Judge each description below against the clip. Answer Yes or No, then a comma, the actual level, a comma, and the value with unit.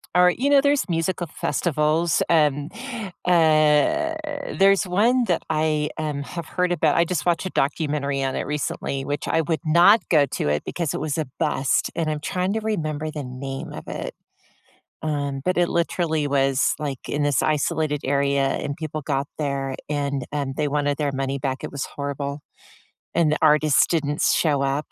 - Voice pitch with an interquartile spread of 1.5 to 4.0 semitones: Yes, average, 3.1 semitones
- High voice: No, medium, 150 Hz